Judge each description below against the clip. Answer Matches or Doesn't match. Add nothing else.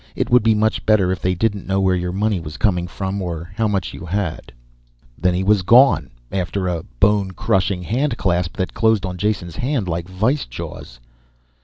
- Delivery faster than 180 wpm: Matches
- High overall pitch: Doesn't match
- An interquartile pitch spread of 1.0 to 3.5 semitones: Matches